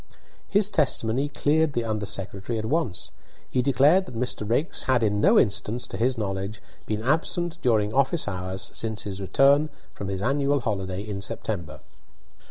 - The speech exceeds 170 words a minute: No, average, 165 wpm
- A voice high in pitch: No, low, 115 Hz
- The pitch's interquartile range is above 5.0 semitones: Yes, wide, 5.5 semitones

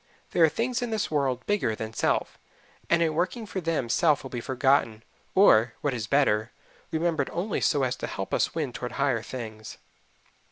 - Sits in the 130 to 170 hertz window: Yes, medium, 140 Hz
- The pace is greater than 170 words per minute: Yes, average, 190 wpm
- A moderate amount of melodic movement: No, wide, 6.0 semitones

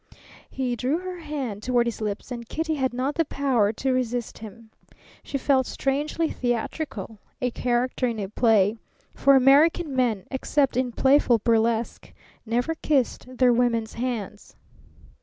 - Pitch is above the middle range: Yes, very high, 250 Hz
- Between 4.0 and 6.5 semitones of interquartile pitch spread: No, average, 3.2 semitones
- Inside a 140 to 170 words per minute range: Yes, average, 145 wpm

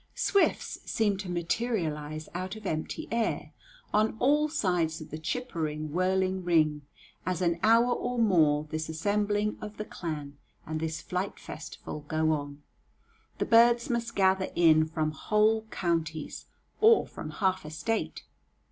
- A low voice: No, medium, 180 Hz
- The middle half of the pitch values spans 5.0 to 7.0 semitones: Yes, wide, 5.5 semitones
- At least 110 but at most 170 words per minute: Yes, average, 145 wpm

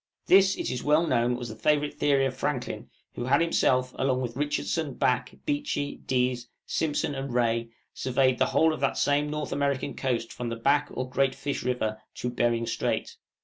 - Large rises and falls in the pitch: No, average, 2.9 semitones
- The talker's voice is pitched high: No, low, 130 Hz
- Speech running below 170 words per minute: No, average, 190 wpm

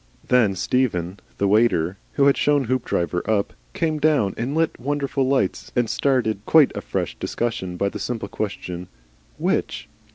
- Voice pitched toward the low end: Yes, low, 120 Hz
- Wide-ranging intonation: Yes, wide, 5.7 semitones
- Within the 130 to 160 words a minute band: Yes, average, 155 wpm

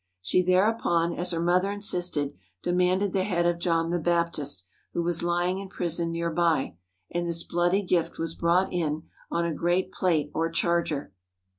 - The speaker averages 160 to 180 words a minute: Yes, average, 175 wpm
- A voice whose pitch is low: No, medium, 170 Hz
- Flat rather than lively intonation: Yes, narrow, 1.5 semitones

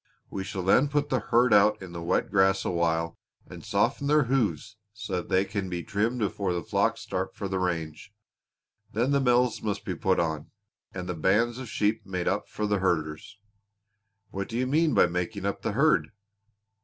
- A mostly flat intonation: No, average, 4.6 semitones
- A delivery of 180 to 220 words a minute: Yes, average, 195 wpm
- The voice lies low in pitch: Yes, low, 100 Hz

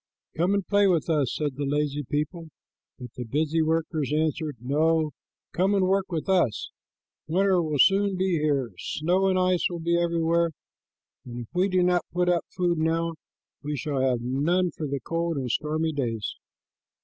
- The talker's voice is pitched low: No, medium, 160 Hz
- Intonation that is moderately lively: Yes, average, 3.3 semitones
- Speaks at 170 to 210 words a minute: Yes, average, 175 wpm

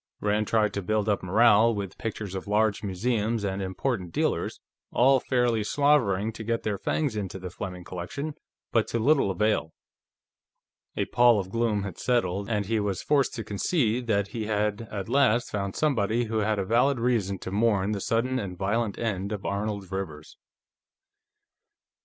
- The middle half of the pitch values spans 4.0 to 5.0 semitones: No, average, 3.0 semitones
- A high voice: No, low, 105 Hz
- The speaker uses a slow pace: No, average, 170 wpm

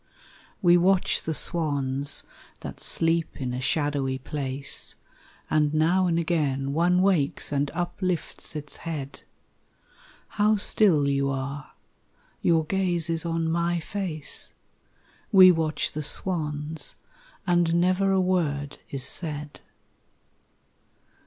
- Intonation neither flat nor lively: Yes, average, 3.5 semitones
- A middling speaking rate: No, slow, 115 wpm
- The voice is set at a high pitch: No, medium, 160 Hz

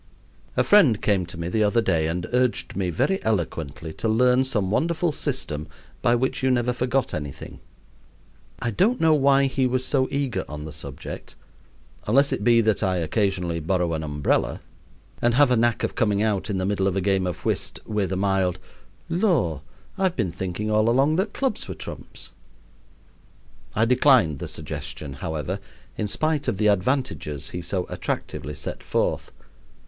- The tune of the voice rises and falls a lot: Yes, wide, 6.9 semitones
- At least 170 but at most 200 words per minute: Yes, average, 175 wpm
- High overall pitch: No, low, 105 Hz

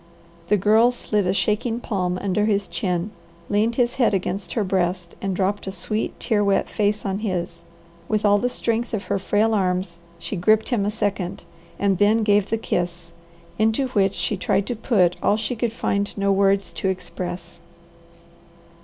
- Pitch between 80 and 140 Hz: No, high, 200 Hz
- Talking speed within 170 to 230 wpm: Yes, average, 180 wpm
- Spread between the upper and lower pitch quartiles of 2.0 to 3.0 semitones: Yes, narrow, 2.6 semitones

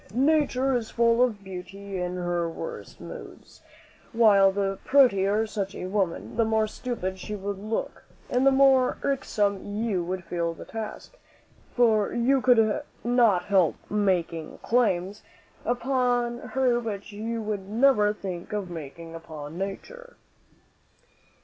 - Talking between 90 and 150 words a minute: Yes, slow, 135 wpm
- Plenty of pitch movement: No, average, 4.3 semitones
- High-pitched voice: Yes, high, 210 Hz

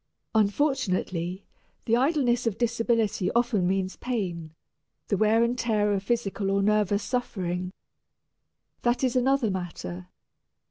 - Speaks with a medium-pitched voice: No, high, 210 Hz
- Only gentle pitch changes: No, average, 4.2 semitones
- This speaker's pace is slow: Yes, slow, 120 wpm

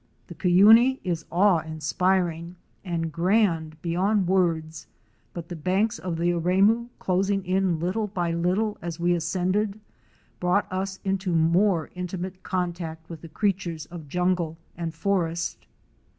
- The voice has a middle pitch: Yes, medium, 180 Hz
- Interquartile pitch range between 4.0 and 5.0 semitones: No, narrow, 2.5 semitones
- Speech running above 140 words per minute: No, slow, 135 wpm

